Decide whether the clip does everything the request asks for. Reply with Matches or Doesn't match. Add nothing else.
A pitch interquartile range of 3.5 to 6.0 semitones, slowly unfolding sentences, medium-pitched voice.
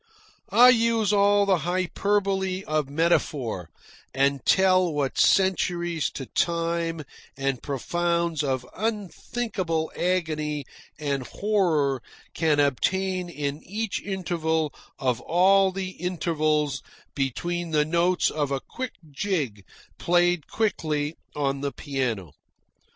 Matches